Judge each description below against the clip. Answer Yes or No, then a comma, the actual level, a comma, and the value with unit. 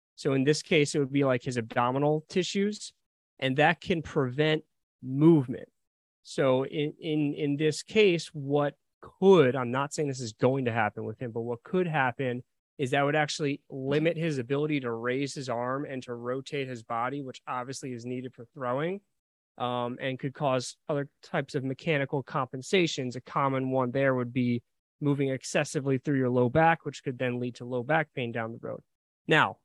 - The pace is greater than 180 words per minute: Yes, average, 190 wpm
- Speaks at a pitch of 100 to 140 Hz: Yes, low, 135 Hz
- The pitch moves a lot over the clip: No, average, 3.3 semitones